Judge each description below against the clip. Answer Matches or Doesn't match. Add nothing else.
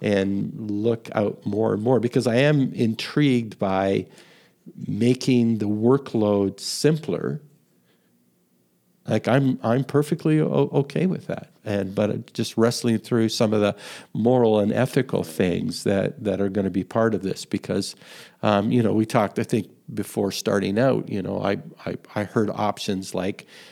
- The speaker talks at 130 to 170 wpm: Matches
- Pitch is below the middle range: Matches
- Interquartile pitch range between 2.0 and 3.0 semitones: Doesn't match